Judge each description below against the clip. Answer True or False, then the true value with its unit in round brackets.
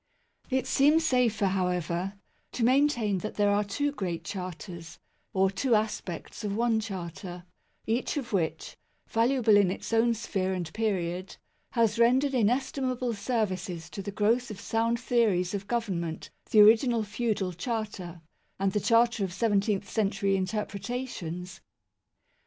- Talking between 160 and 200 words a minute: False (140 wpm)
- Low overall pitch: False (210 Hz)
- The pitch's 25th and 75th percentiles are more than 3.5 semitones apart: True (3.9 semitones)